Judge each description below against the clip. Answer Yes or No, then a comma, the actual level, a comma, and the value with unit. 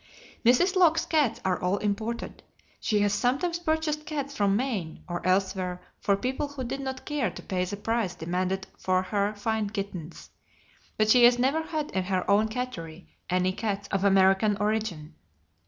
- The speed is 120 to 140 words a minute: No, average, 170 wpm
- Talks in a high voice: Yes, high, 210 Hz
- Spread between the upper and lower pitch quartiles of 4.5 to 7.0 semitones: Yes, wide, 5.4 semitones